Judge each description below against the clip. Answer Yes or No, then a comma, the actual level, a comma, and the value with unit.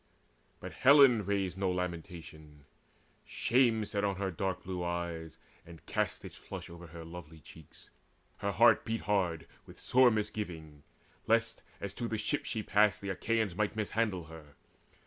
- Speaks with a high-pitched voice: No, very low, 95 Hz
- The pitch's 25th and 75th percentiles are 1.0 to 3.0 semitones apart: No, average, 4.3 semitones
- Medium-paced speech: Yes, average, 155 wpm